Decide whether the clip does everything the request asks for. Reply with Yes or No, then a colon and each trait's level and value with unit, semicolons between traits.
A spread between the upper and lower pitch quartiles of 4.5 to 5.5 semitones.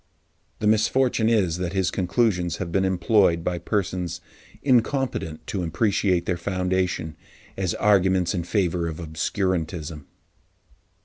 No: average, 3.0 semitones